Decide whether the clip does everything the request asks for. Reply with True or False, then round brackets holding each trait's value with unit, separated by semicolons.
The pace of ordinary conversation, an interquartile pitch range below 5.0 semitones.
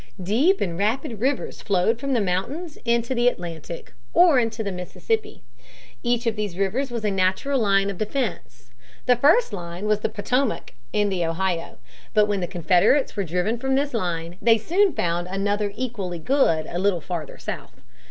False (175 wpm; 5.6 semitones)